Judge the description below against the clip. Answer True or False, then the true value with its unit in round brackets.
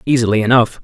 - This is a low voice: True (115 Hz)